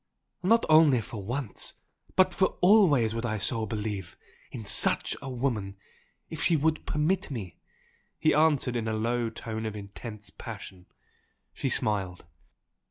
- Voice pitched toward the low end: Yes, low, 115 Hz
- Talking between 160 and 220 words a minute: No, average, 145 wpm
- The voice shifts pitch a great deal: Yes, wide, 6.1 semitones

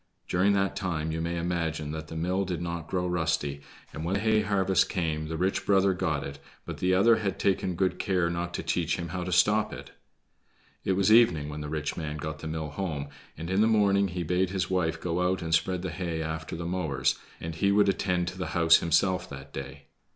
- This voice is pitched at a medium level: No, very low, 90 Hz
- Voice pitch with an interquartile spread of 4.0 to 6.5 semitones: No, average, 2.9 semitones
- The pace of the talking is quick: Yes, fast, 225 wpm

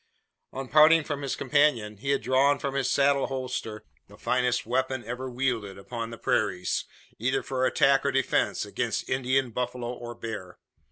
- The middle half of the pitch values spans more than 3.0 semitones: No, narrow, 2.6 semitones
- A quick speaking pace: No, average, 165 wpm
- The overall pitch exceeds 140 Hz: No, low, 130 Hz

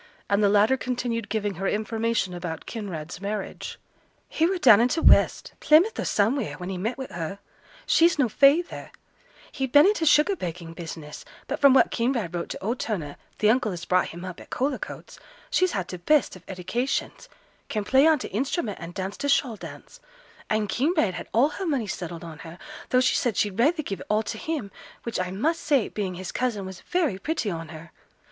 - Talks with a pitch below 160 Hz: No, high, 215 Hz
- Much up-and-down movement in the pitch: Yes, wide, 6.8 semitones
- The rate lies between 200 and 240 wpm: Yes, fast, 205 wpm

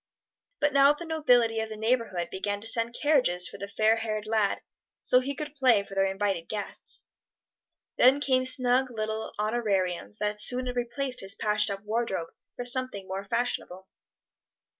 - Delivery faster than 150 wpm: Yes, average, 160 wpm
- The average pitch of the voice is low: No, high, 225 Hz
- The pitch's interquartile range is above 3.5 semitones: Yes, average, 4.0 semitones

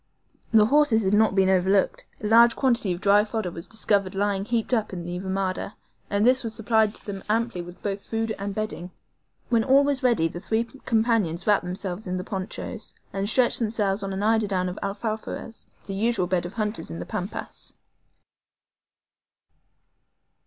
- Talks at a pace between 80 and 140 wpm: No, average, 170 wpm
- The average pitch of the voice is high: Yes, high, 205 Hz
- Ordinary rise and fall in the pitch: Yes, average, 3.0 semitones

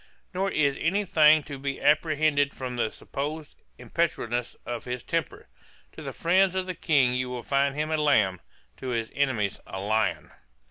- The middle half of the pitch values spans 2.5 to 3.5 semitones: No, average, 4.2 semitones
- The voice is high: No, medium, 140 Hz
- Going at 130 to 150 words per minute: No, average, 175 wpm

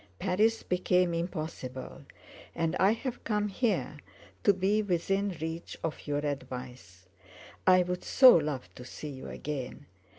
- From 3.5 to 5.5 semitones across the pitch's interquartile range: Yes, average, 5.1 semitones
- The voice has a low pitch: No, medium, 170 Hz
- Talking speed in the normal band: No, slow, 130 wpm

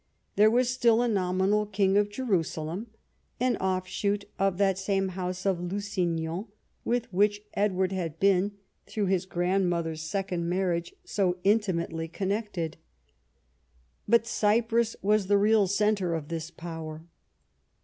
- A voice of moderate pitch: No, high, 195 Hz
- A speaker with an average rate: No, slow, 130 wpm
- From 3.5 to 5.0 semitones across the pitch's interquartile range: No, average, 2.9 semitones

